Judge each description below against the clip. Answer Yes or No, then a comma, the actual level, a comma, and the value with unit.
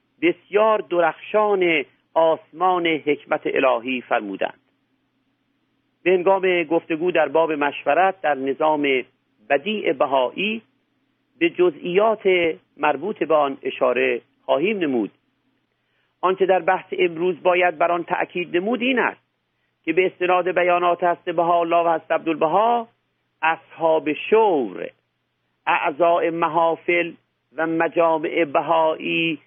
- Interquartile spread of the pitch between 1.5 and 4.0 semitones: Yes, average, 2.7 semitones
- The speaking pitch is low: No, medium, 170 Hz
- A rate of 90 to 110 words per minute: Yes, slow, 105 wpm